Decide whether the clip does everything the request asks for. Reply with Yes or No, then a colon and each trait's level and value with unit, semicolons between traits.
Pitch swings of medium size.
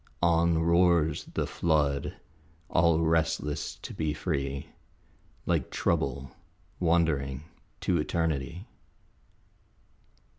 Yes: average, 3.1 semitones